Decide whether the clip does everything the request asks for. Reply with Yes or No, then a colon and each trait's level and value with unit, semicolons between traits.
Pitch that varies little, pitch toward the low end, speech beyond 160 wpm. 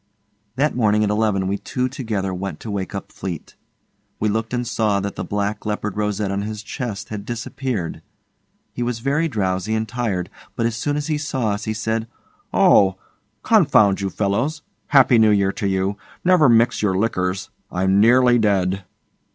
No: average, 3.6 semitones; low, 105 Hz; average, 175 wpm